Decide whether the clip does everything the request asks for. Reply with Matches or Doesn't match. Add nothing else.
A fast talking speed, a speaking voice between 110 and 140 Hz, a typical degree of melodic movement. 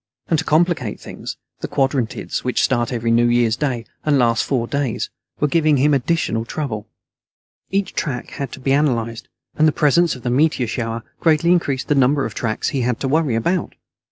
Doesn't match